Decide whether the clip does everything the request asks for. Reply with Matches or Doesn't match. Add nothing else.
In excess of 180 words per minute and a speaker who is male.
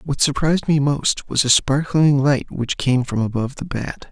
Matches